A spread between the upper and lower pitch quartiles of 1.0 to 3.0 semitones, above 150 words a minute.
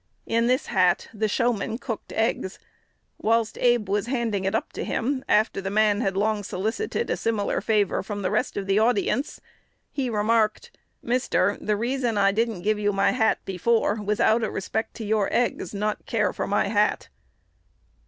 Yes: narrow, 2.4 semitones; average, 180 wpm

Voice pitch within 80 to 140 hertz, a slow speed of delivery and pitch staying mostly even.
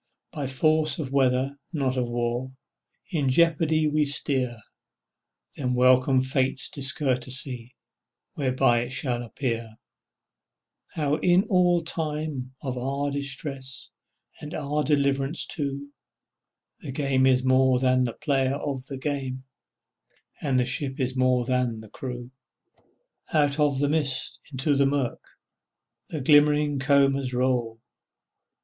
Yes: low, 135 Hz; slow, 125 wpm; narrow, 2.3 semitones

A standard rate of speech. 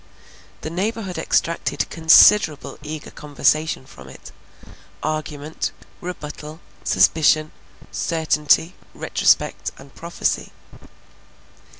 No: slow, 75 wpm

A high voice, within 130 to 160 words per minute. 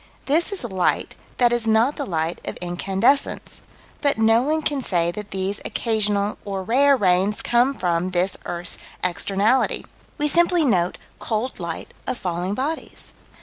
Yes: high, 210 Hz; average, 150 wpm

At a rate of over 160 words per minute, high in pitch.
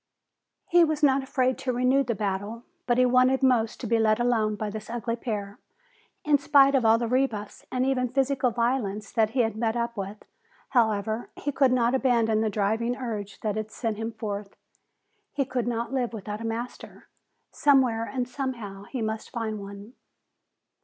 Yes: average, 180 wpm; high, 235 Hz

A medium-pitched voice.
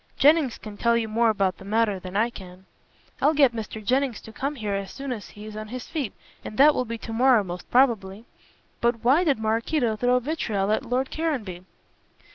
No: high, 230 Hz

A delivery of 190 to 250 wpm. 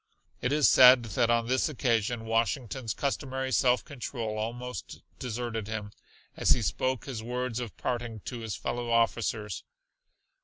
No: average, 145 wpm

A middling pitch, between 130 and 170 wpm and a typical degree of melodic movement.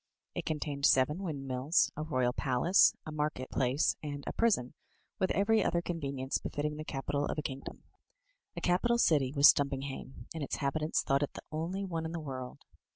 No: medium, 145 Hz; average, 180 wpm; average, 3.2 semitones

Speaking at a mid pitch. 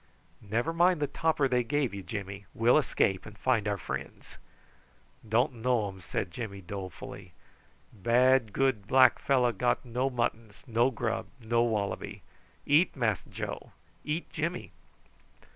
No: low, 120 Hz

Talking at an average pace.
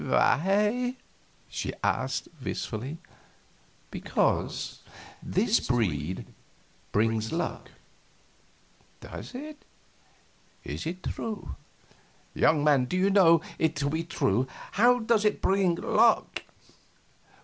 No: slow, 95 wpm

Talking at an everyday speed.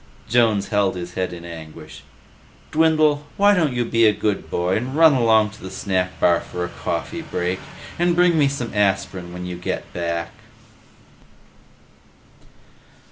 Yes: average, 155 wpm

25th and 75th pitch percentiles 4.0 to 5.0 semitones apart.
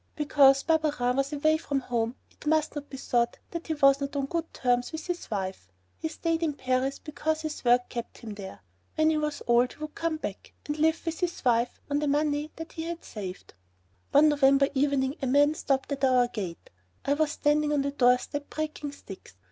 No: average, 3.6 semitones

